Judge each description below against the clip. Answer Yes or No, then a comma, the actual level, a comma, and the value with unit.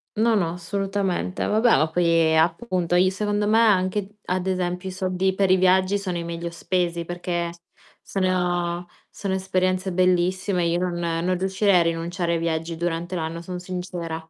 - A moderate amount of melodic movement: No, narrow, 1.8 semitones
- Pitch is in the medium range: Yes, medium, 180 Hz